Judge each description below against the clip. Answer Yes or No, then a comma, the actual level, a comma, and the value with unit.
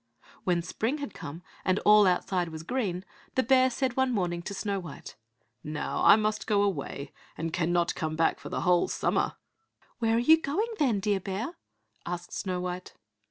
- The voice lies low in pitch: No, high, 195 Hz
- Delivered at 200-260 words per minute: No, average, 180 wpm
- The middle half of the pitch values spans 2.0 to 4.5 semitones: No, average, 5.2 semitones